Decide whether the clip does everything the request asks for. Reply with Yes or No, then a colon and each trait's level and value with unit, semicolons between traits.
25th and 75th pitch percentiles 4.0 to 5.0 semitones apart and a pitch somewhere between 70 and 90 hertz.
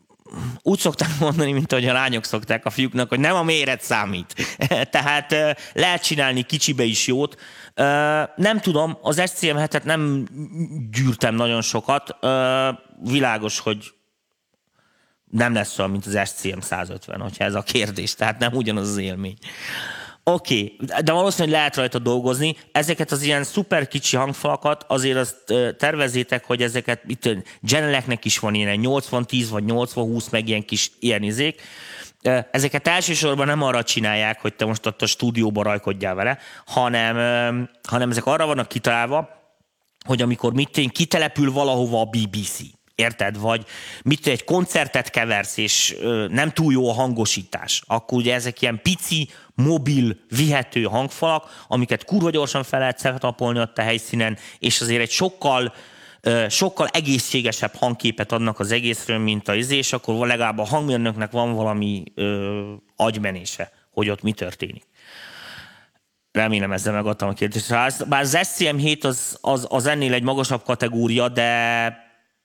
No: average, 4.4 semitones; low, 125 Hz